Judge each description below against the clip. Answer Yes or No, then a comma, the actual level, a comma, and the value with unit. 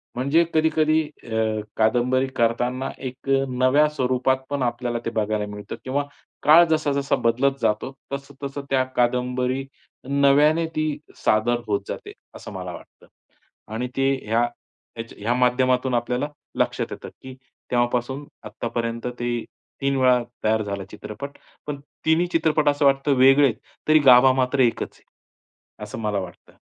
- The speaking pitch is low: Yes, low, 130 Hz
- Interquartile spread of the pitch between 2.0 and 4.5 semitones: Yes, average, 2.8 semitones